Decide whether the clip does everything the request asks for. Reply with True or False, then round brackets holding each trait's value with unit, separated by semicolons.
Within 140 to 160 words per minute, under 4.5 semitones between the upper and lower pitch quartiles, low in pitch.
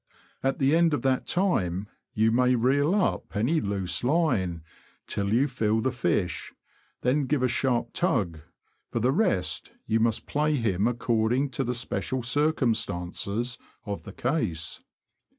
False (150 wpm; 5.0 semitones; 120 Hz)